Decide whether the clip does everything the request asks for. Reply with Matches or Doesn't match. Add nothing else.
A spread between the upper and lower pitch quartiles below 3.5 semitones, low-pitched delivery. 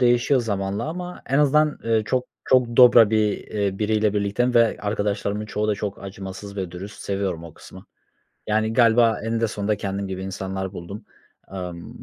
Matches